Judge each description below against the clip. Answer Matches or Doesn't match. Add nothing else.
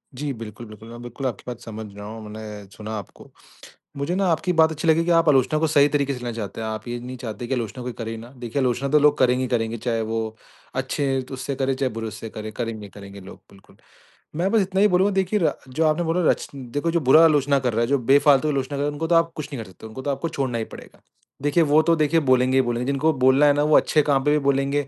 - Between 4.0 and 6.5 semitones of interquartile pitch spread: Matches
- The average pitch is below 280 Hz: Matches